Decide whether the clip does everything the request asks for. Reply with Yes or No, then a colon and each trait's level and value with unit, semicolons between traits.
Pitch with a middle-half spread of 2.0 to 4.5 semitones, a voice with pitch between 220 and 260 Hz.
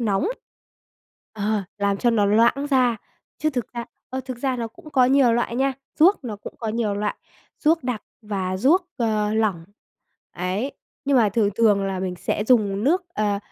Yes: average, 4.1 semitones; high, 230 Hz